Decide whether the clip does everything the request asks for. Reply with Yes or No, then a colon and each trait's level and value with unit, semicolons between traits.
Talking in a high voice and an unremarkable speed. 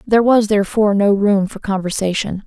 Yes: high, 205 Hz; average, 170 wpm